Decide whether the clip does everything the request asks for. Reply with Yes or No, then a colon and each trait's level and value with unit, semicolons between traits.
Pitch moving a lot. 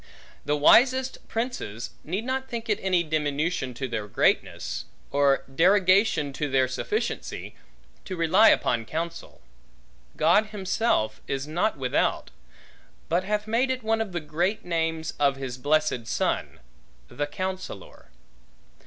Yes: wide, 7.1 semitones